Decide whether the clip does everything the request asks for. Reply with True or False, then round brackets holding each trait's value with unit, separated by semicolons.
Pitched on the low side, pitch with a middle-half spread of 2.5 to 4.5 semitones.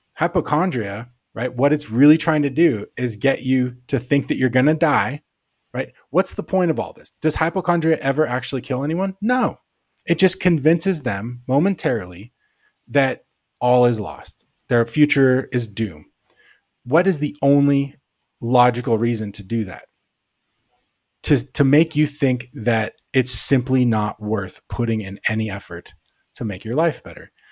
False (130 Hz; 4.9 semitones)